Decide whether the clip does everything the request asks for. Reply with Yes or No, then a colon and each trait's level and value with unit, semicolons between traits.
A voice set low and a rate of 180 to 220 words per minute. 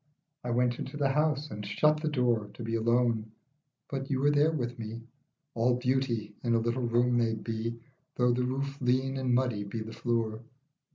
Yes: low, 120 Hz; average, 190 wpm